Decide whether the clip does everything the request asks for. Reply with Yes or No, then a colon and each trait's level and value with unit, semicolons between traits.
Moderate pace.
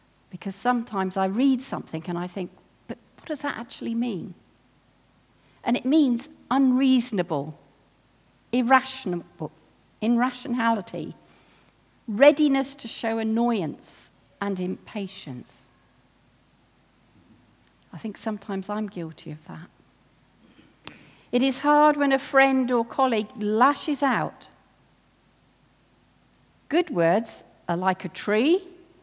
No: slow, 100 wpm